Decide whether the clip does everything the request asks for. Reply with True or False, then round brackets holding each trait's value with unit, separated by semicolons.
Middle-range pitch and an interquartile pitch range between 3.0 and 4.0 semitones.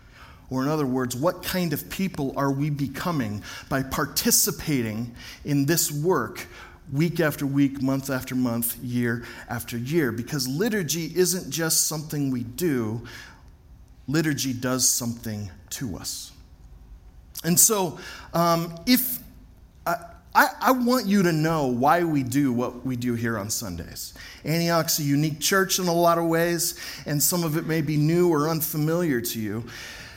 False (145 Hz; 5.6 semitones)